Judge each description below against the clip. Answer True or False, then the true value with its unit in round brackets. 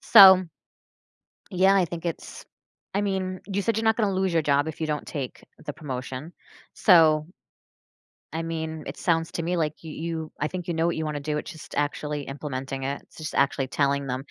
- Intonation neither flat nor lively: True (3.6 semitones)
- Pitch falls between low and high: True (160 Hz)